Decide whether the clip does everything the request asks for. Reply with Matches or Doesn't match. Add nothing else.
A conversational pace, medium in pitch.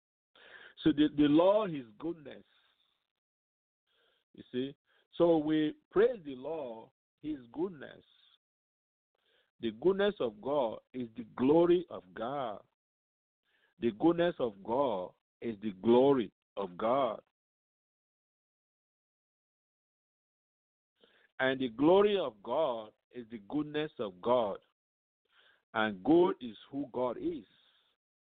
Doesn't match